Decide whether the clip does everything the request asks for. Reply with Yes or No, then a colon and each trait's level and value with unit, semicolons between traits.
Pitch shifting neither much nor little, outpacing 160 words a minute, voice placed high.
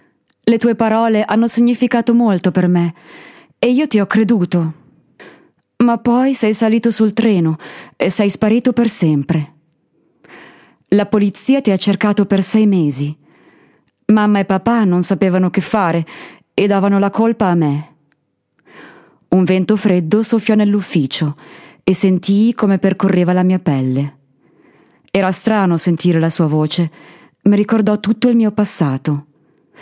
No: average, 4.6 semitones; average, 140 wpm; high, 195 Hz